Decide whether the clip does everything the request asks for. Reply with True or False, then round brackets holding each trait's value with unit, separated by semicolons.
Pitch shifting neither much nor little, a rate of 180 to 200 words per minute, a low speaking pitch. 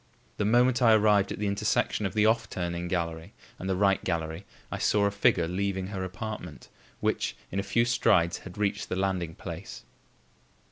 True (3.1 semitones; 185 wpm; 95 Hz)